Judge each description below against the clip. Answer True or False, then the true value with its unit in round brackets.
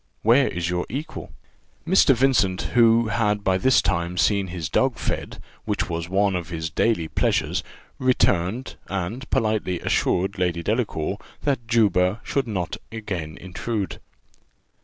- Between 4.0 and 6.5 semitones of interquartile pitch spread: True (4.7 semitones)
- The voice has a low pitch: True (100 Hz)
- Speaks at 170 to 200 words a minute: False (140 wpm)